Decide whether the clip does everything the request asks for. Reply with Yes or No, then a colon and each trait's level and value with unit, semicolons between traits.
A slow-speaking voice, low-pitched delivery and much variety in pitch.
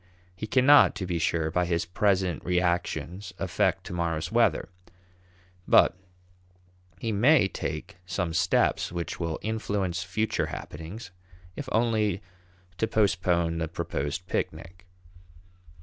No: slow, 120 wpm; very low, 90 Hz; average, 3.8 semitones